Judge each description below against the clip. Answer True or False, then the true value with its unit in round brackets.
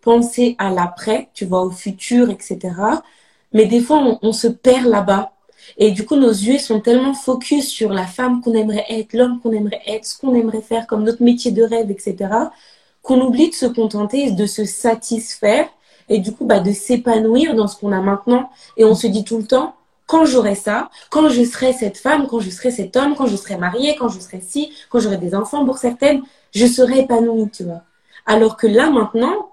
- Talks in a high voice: True (230 Hz)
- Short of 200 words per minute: False (215 wpm)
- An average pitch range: True (3.4 semitones)